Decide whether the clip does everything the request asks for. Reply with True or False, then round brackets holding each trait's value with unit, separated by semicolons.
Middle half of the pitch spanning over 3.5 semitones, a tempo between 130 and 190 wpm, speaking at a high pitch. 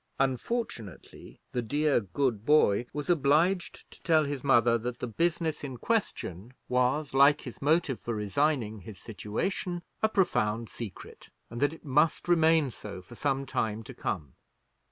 False (5.4 semitones; 155 wpm; 135 Hz)